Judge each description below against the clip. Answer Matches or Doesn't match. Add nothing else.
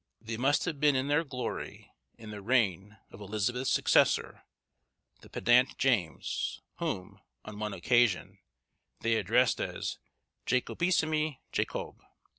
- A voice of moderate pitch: Doesn't match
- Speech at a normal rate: Doesn't match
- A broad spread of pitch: Doesn't match